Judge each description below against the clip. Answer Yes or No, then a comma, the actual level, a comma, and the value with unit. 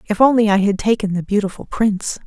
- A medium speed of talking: No, fast, 210 wpm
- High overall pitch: Yes, high, 205 Hz